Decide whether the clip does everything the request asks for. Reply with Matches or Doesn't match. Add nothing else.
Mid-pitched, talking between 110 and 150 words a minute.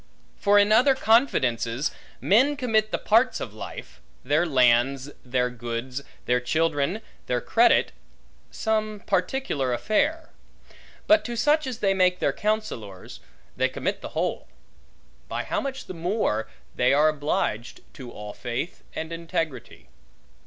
Matches